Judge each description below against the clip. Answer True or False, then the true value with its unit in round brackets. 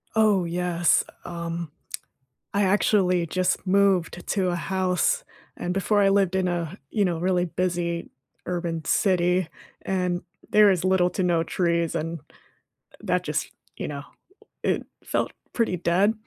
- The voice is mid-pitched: True (180 Hz)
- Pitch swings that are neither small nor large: False (1.9 semitones)